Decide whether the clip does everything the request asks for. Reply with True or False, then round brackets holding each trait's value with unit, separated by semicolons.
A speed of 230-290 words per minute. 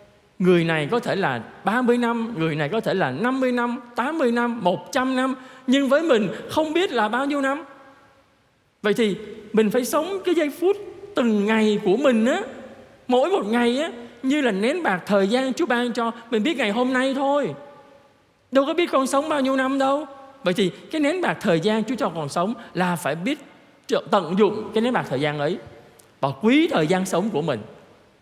False (205 wpm)